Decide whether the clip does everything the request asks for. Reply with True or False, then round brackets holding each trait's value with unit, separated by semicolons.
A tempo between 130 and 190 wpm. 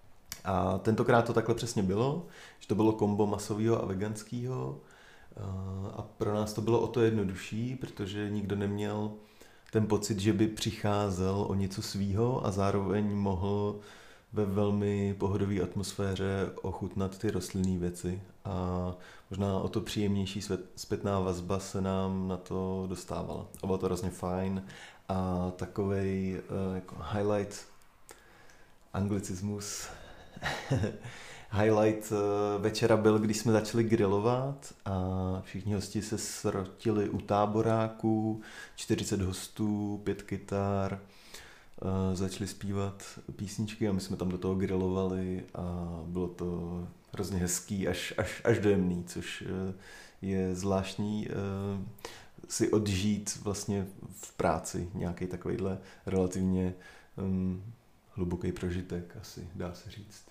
False (120 wpm)